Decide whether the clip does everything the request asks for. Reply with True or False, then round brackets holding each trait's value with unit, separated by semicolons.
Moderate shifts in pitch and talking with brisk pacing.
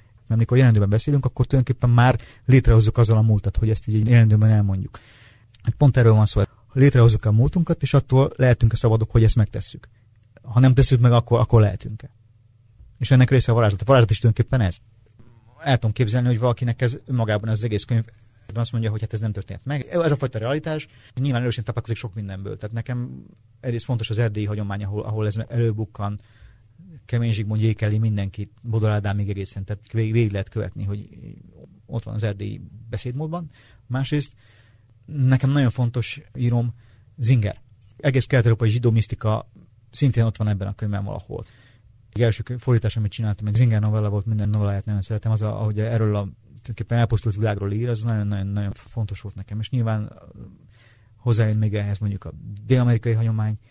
False (2.0 semitones; 180 wpm)